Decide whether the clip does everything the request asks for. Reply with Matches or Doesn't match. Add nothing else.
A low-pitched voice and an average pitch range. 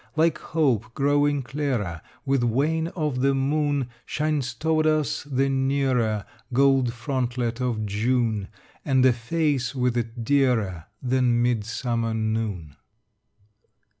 Matches